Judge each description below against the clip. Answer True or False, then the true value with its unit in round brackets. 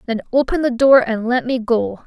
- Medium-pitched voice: False (245 Hz)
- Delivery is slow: False (230 wpm)